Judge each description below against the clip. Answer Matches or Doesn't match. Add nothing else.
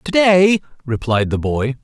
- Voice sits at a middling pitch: Matches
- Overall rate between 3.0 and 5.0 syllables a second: Matches